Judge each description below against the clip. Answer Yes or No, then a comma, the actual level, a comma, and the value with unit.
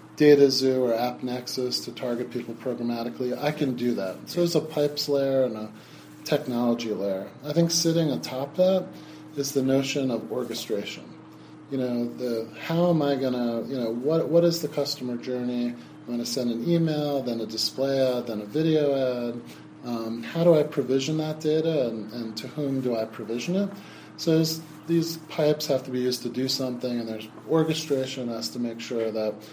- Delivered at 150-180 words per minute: No, average, 195 wpm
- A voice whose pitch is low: Yes, low, 130 Hz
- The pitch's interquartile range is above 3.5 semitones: Yes, average, 4.2 semitones